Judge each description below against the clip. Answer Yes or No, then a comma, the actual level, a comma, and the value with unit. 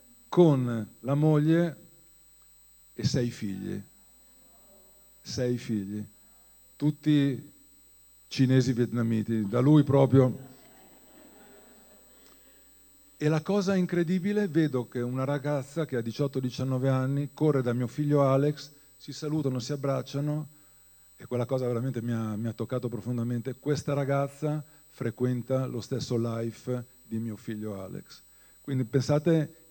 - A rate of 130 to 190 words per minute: No, slow, 115 wpm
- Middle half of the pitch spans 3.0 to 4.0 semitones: Yes, average, 3.6 semitones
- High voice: No, low, 135 Hz